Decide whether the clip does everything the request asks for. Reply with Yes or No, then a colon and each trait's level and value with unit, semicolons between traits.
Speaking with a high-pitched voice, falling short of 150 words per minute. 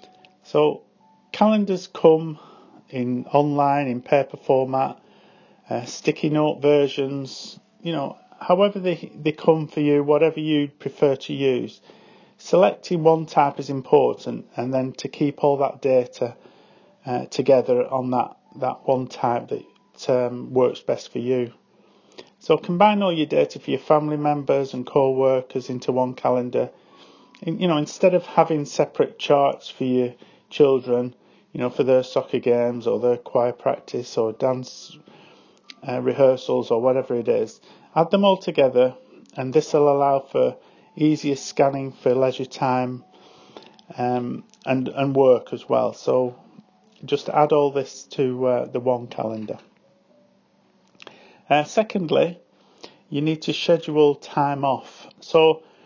No: medium, 140 Hz; average, 140 wpm